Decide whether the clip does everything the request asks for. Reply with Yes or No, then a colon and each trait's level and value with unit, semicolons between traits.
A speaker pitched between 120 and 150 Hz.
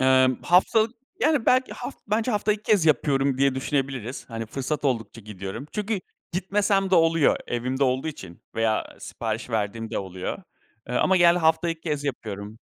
Yes: medium, 140 Hz